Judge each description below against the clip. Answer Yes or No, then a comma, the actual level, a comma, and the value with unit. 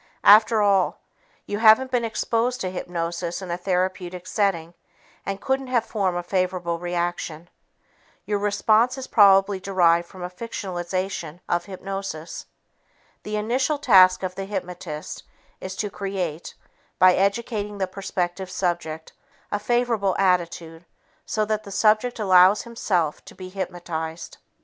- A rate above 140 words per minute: No, slow, 135 wpm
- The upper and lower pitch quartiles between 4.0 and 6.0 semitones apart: No, average, 3.1 semitones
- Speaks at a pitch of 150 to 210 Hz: Yes, high, 190 Hz